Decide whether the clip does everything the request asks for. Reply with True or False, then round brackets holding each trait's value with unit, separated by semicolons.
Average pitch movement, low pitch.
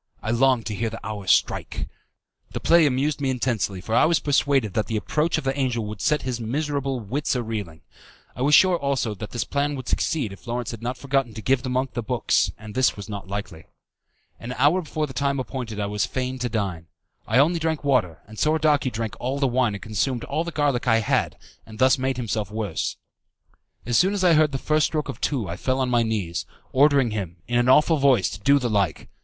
True (4.5 semitones; 125 Hz)